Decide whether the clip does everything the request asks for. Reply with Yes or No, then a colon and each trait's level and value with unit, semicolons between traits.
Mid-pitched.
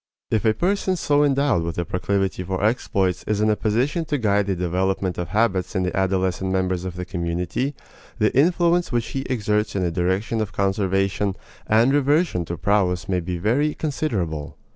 No: low, 100 Hz